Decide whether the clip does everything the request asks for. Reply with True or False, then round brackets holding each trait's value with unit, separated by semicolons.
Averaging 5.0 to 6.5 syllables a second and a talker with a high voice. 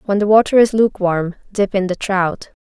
True (5.3 syllables/s; 200 Hz)